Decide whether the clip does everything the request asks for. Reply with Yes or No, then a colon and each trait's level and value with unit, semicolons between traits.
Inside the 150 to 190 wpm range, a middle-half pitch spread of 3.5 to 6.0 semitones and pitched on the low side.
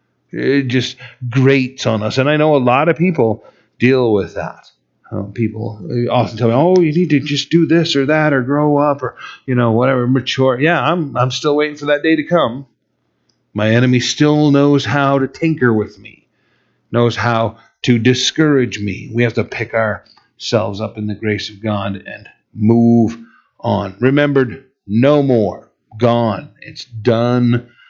Yes: average, 175 wpm; average, 4.1 semitones; low, 125 Hz